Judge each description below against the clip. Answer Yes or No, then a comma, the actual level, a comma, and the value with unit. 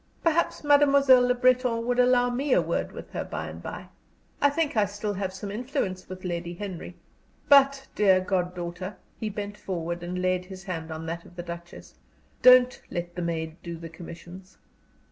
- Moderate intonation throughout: No, wide, 6.2 semitones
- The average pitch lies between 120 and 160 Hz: No, high, 190 Hz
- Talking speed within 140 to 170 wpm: No, average, 185 wpm